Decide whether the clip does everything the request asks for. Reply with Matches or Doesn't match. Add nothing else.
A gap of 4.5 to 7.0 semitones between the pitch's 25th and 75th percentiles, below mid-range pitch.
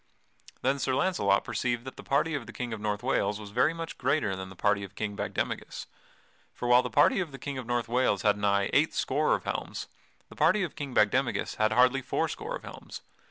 Matches